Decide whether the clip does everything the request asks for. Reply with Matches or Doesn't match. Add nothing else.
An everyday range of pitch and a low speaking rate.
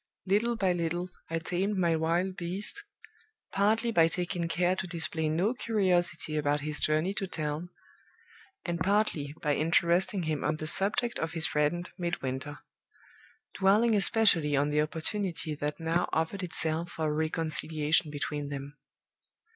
Doesn't match